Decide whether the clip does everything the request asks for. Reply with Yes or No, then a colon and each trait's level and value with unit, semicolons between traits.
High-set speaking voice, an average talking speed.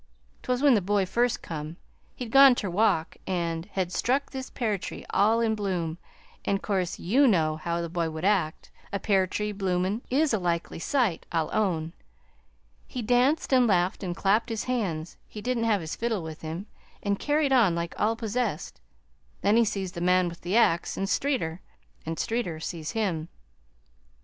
Yes: high, 195 Hz; average, 185 wpm